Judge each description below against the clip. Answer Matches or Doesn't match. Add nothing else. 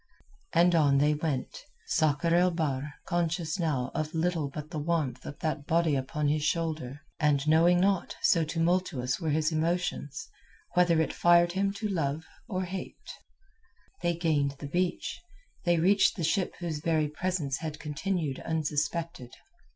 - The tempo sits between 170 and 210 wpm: Doesn't match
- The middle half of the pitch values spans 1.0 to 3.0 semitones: Matches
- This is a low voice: Doesn't match